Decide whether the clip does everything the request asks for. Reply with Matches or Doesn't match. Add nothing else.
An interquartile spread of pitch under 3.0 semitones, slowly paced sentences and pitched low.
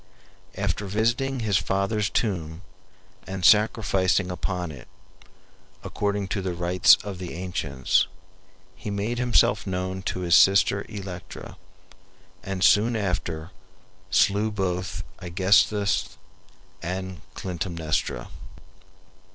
Matches